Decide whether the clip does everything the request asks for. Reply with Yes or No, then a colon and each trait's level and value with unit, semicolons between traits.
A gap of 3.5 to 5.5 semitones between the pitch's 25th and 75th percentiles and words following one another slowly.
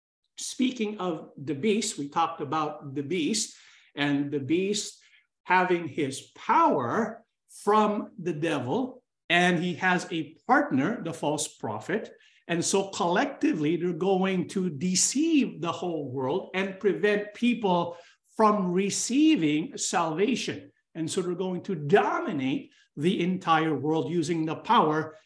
Yes: average, 5.2 semitones; slow, 130 wpm